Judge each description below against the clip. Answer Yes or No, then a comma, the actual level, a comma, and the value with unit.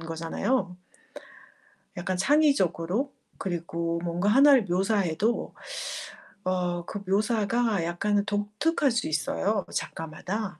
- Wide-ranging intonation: No, average, 4.5 semitones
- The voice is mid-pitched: No, high, 195 Hz